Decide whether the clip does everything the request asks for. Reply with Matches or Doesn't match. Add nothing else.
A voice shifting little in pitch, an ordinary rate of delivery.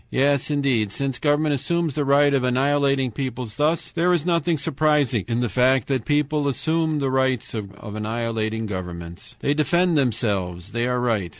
Doesn't match